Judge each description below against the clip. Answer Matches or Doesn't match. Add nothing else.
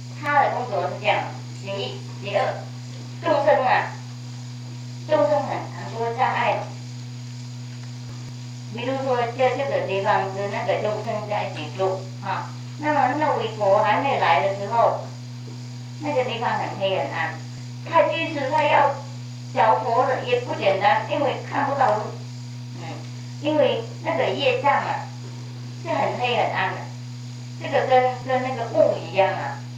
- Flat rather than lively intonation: Matches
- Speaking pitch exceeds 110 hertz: Matches